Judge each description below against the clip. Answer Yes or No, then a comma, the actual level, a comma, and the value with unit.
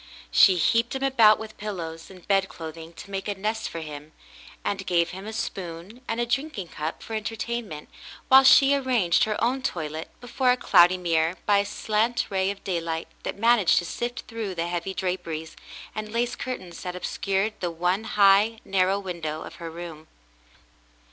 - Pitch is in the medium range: No, high, 195 Hz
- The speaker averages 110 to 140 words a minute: No, average, 175 wpm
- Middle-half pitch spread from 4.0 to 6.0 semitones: Yes, average, 4.8 semitones